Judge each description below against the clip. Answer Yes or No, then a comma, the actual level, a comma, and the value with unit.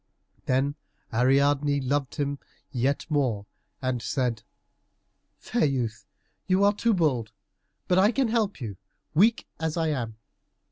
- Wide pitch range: Yes, wide, 5.9 semitones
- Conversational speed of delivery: No, slow, 130 wpm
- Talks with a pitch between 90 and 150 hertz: Yes, medium, 140 Hz